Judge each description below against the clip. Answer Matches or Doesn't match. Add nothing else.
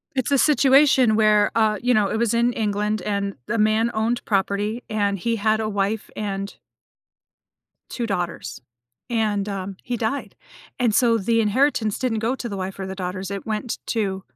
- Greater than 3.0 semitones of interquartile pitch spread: Doesn't match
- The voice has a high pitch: Matches